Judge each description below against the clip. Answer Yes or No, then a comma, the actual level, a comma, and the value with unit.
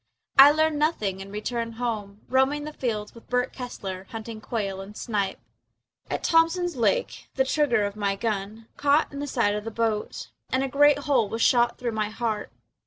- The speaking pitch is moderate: No, high, 230 Hz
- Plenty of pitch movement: No, average, 5.0 semitones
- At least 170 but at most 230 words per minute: Yes, average, 185 wpm